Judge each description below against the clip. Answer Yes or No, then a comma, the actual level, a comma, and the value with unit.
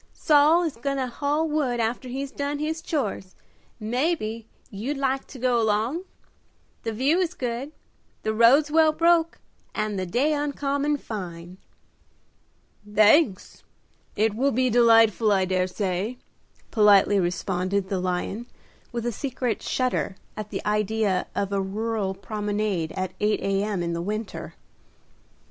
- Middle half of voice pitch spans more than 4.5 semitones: Yes, wide, 5.6 semitones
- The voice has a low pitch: No, high, 225 Hz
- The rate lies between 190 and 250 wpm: No, average, 140 wpm